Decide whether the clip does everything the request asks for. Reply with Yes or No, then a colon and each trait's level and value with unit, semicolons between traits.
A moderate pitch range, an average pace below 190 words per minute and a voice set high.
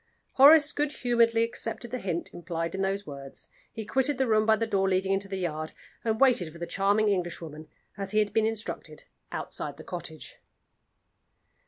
Yes: average, 4.8 semitones; average, 180 wpm; high, 200 Hz